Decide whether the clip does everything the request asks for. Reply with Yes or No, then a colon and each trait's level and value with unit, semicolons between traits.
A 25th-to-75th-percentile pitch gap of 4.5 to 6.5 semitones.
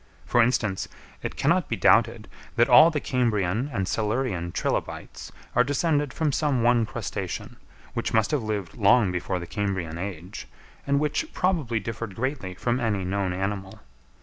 Yes: average, 5.3 semitones